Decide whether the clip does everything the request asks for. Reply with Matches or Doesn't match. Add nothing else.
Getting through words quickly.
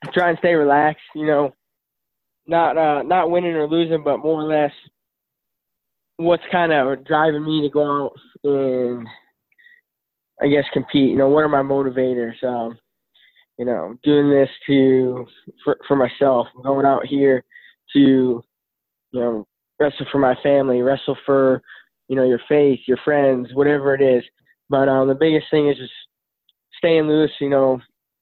Doesn't match